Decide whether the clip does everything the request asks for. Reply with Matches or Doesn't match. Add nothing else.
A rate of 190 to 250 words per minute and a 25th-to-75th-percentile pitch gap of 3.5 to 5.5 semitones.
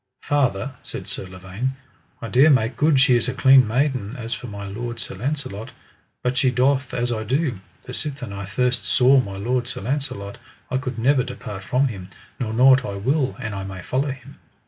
Matches